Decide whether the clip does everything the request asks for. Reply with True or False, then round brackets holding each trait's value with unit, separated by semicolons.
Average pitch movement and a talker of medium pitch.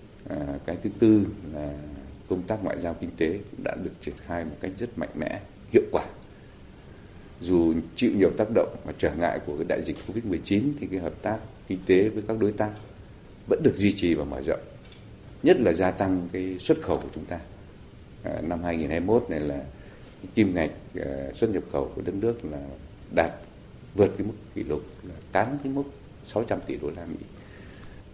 False (4.7 semitones; 90 Hz)